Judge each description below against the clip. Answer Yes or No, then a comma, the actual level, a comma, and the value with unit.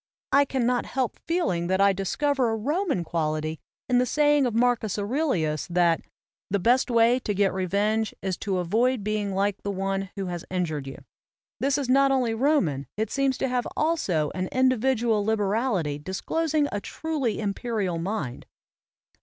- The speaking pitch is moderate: No, high, 215 Hz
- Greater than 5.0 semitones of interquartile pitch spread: Yes, wide, 5.6 semitones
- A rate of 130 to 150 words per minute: No, average, 165 wpm